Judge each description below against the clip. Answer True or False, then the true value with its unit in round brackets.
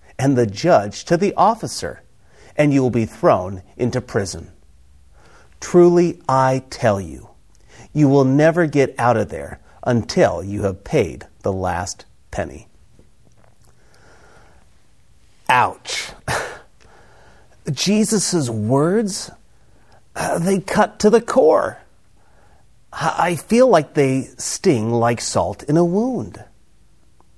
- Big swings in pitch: True (8.9 semitones)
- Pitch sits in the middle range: False (130 Hz)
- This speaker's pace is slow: True (110 wpm)